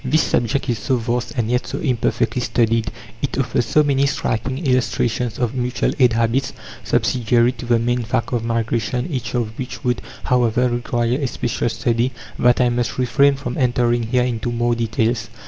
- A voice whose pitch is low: Yes, low, 120 Hz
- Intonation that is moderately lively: No, narrow, 1.4 semitones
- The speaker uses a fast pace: No, average, 180 wpm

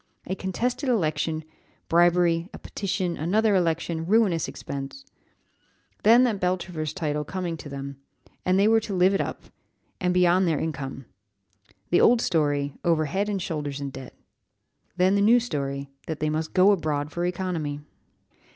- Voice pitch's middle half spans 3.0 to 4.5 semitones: Yes, average, 4.2 semitones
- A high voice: No, medium, 175 Hz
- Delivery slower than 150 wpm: No, average, 160 wpm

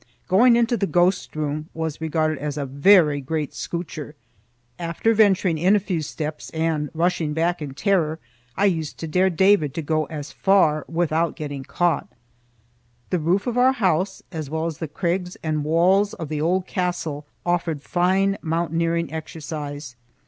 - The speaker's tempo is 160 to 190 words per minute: Yes, average, 165 wpm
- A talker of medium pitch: Yes, medium, 165 Hz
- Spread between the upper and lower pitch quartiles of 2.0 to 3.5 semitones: Yes, average, 3.2 semitones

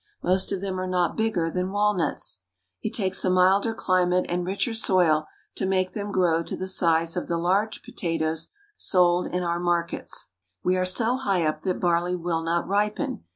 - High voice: No, medium, 180 Hz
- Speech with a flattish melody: Yes, narrow, 2.0 semitones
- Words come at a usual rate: Yes, average, 185 wpm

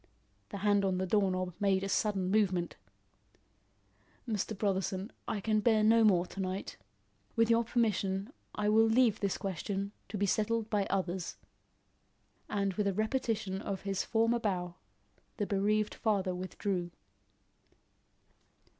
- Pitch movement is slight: Yes, narrow, 2.3 semitones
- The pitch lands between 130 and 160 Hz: No, high, 200 Hz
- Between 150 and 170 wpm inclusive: No, average, 140 wpm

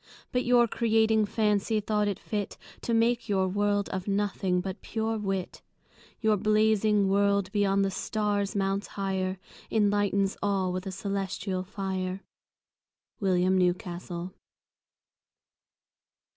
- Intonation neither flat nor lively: No, narrow, 1.9 semitones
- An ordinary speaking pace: No, slow, 115 wpm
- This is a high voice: Yes, high, 200 Hz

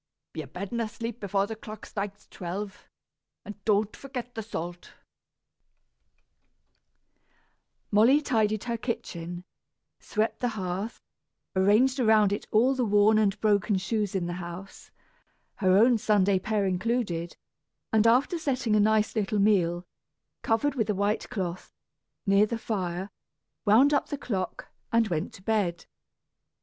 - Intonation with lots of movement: No, average, 3.2 semitones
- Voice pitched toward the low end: No, high, 210 Hz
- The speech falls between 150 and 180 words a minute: No, slow, 135 wpm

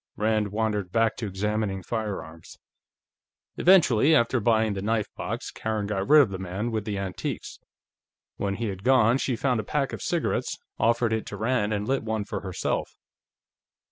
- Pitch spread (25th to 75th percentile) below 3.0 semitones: Yes, narrow, 2.6 semitones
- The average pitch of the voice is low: Yes, low, 110 Hz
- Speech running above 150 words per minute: Yes, average, 175 wpm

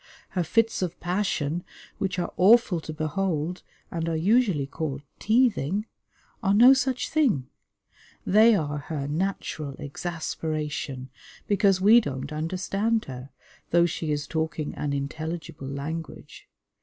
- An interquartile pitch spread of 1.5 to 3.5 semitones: No, average, 5.1 semitones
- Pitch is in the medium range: Yes, medium, 165 Hz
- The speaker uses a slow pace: Yes, slow, 125 wpm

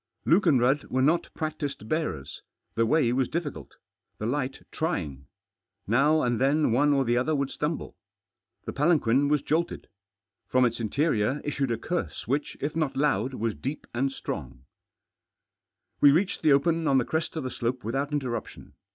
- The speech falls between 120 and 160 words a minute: No, average, 170 wpm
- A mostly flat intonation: No, average, 4.2 semitones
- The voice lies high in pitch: No, medium, 140 Hz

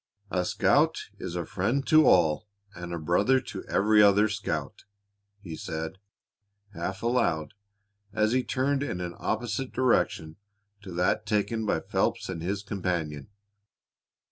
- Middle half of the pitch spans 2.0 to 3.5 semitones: No, average, 4.3 semitones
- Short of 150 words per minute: Yes, average, 140 wpm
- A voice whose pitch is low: Yes, low, 100 Hz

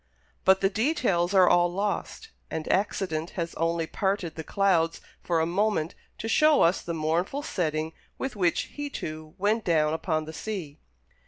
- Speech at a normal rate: Yes, average, 165 wpm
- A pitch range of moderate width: Yes, average, 4.0 semitones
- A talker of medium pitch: Yes, medium, 175 Hz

